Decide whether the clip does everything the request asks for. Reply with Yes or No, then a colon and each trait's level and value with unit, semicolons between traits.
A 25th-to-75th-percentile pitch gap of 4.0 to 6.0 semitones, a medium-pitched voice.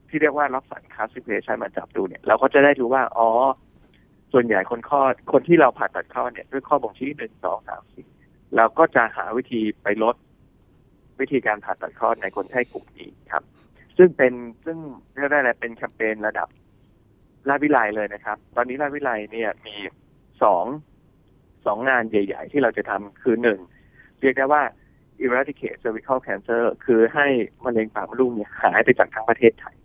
No: average, 4.3 semitones; low, 120 Hz